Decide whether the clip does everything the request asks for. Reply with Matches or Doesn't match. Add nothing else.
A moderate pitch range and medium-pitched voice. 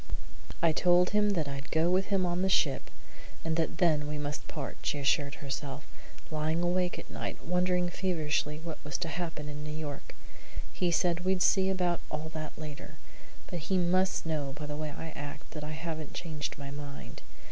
Matches